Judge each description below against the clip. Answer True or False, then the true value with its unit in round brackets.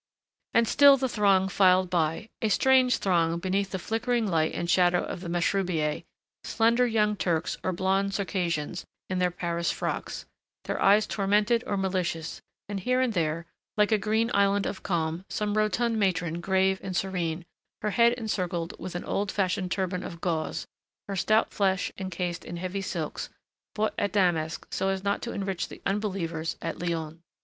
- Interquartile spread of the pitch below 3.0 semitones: False (3.3 semitones)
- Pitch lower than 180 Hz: False (190 Hz)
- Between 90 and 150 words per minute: False (170 wpm)